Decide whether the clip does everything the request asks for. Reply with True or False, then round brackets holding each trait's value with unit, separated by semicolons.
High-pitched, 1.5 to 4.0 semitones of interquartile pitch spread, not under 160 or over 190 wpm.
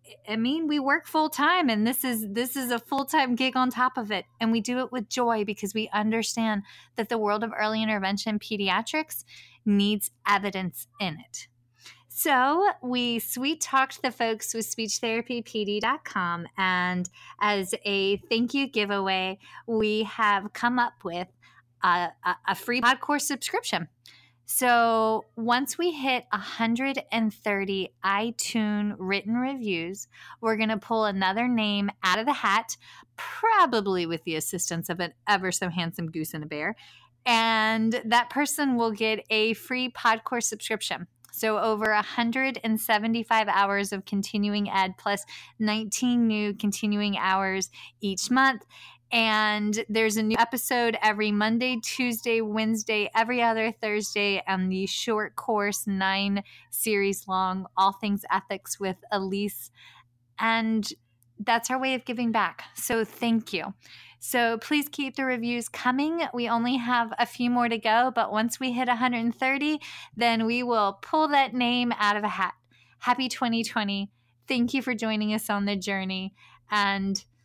False (220 Hz; 3.4 semitones; 145 wpm)